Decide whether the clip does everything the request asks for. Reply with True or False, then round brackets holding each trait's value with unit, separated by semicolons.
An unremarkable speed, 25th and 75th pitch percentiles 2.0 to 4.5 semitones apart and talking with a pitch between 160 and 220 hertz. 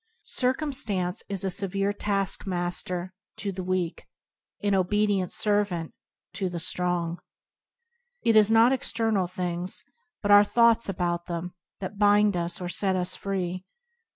False (130 wpm; 2.6 semitones; 190 Hz)